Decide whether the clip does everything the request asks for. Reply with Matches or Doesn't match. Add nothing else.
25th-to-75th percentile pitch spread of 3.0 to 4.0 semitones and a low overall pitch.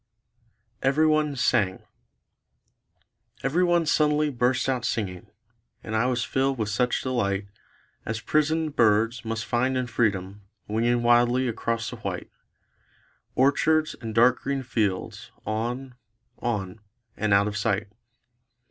Matches